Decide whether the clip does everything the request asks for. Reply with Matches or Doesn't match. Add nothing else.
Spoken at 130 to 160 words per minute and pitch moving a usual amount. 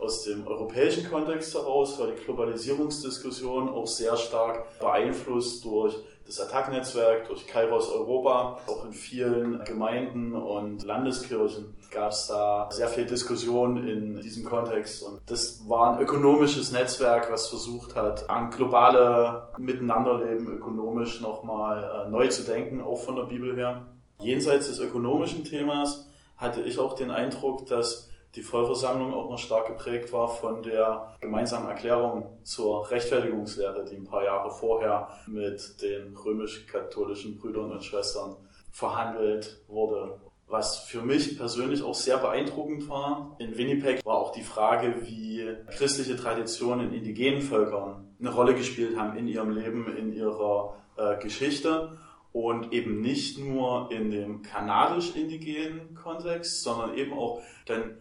Matches